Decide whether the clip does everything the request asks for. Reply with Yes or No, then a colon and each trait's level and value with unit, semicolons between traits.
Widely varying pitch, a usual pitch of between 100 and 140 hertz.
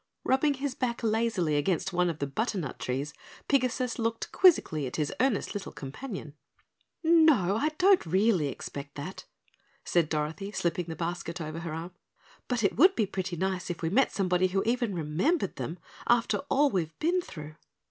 No: wide, 7.2 semitones; high, 190 Hz